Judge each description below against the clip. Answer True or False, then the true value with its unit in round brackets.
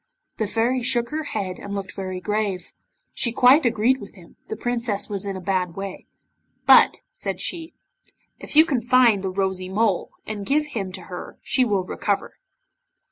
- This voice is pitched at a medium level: False (210 Hz)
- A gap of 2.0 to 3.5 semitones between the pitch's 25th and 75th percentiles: False (4.4 semitones)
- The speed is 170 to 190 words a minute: True (180 wpm)